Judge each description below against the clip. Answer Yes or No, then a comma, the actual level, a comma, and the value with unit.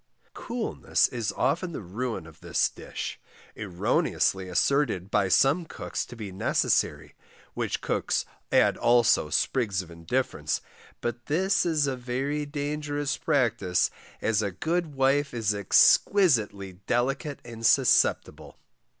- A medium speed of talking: No, slow, 125 wpm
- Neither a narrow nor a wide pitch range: No, wide, 6.2 semitones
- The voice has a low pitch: Yes, low, 125 Hz